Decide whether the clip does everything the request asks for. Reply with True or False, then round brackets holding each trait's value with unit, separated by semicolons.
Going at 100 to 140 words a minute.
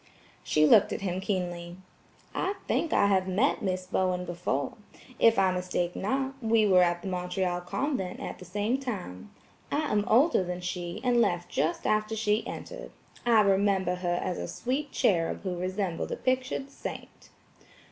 False (165 wpm)